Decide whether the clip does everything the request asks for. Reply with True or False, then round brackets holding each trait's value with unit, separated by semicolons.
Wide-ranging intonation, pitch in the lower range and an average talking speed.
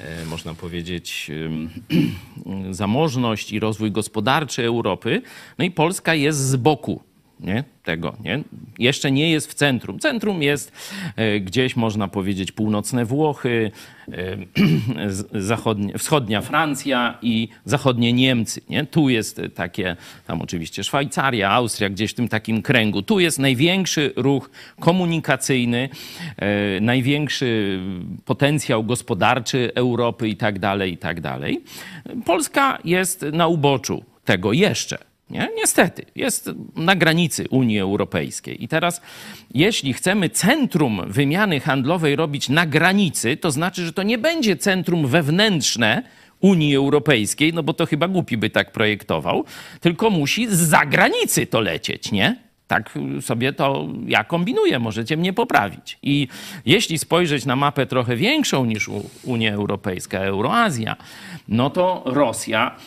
True (7.0 semitones; 130 Hz; 125 wpm)